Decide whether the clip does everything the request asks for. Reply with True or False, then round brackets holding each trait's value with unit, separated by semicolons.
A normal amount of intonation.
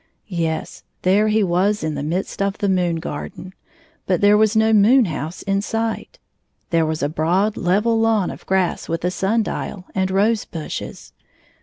True (3.8 semitones)